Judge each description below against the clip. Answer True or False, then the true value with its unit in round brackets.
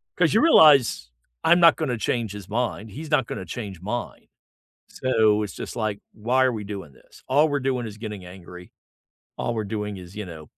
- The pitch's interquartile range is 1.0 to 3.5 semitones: False (4.5 semitones)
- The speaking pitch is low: True (110 Hz)